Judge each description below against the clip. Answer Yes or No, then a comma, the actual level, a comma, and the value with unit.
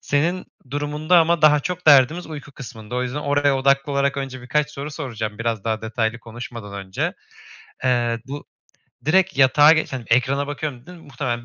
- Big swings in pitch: No, average, 3.9 semitones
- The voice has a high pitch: No, medium, 140 Hz